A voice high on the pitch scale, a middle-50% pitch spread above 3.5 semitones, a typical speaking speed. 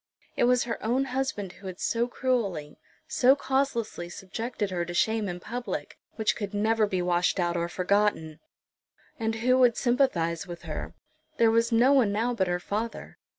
Yes: high, 220 Hz; average, 5.2 semitones; average, 175 wpm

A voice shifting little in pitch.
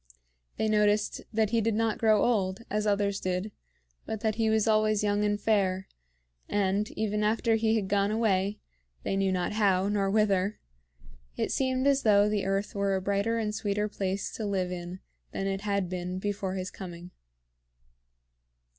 Yes: narrow, 1.9 semitones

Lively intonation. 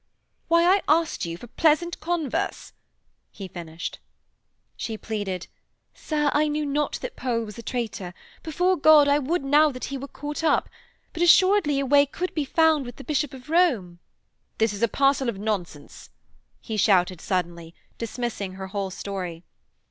Yes: wide, 7.5 semitones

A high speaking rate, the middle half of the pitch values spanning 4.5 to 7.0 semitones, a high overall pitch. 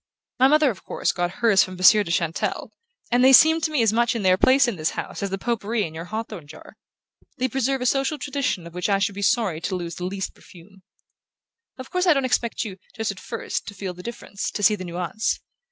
Yes: fast, 245 wpm; average, 5.3 semitones; high, 210 Hz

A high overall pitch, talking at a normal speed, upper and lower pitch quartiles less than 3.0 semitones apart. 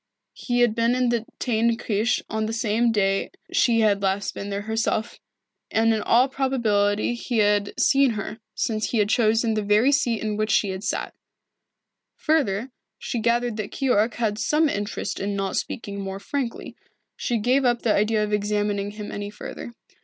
Yes: high, 220 Hz; average, 175 wpm; narrow, 2.6 semitones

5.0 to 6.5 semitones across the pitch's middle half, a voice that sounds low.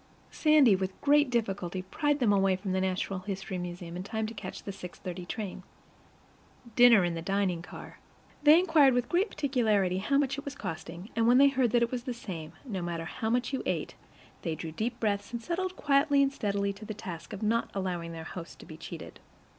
No: wide, 5.6 semitones; high, 205 Hz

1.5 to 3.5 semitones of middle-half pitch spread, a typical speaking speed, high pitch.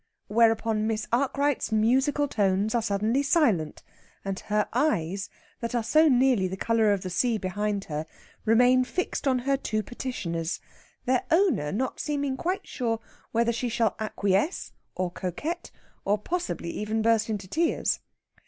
No: average, 4.6 semitones; average, 150 wpm; high, 225 Hz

